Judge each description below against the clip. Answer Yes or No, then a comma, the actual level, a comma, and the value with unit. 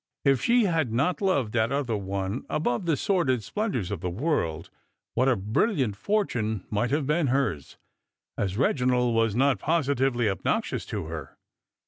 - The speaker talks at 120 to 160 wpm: Yes, average, 155 wpm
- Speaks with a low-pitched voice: Yes, low, 125 Hz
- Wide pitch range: Yes, wide, 5.8 semitones